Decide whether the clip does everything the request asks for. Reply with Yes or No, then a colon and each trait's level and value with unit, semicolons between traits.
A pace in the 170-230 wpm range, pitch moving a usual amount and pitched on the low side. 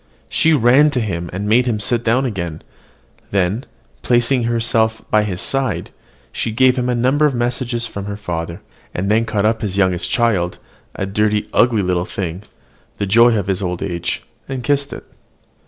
Yes: average, 180 wpm; average, 4.0 semitones; low, 110 Hz